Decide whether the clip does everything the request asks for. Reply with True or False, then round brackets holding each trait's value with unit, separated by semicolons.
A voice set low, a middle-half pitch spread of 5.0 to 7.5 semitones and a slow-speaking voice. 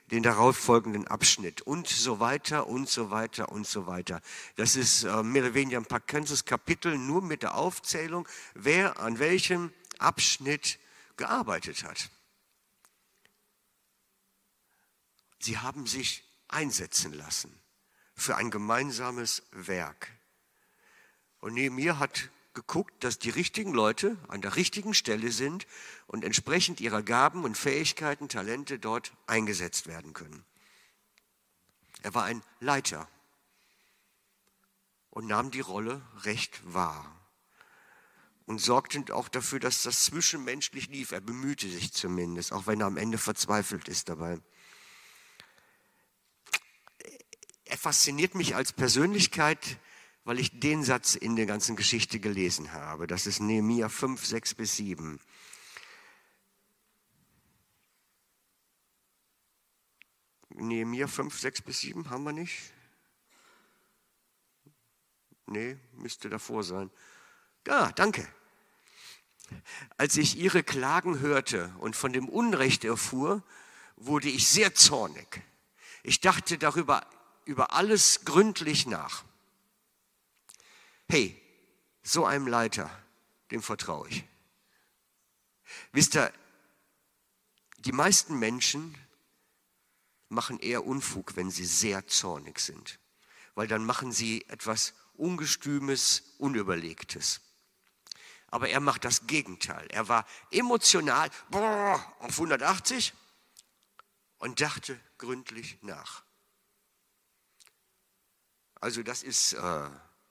True (120 Hz; 5.4 semitones; 105 wpm)